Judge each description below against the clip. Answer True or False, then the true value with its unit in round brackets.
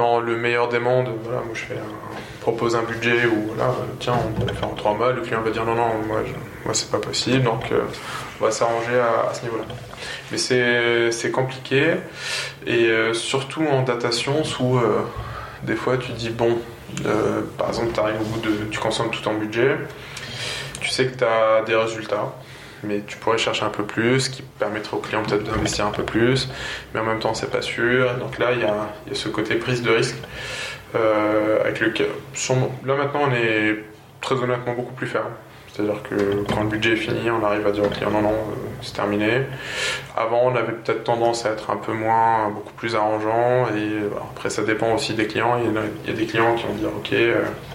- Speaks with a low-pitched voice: True (115 Hz)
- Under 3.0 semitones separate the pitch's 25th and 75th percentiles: True (2.4 semitones)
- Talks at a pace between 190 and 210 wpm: False (220 wpm)